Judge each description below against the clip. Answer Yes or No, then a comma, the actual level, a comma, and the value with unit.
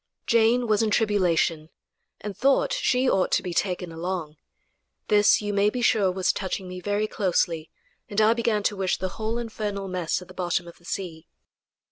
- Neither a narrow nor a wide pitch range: Yes, average, 3.2 semitones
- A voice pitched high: Yes, high, 200 Hz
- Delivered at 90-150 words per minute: No, average, 185 wpm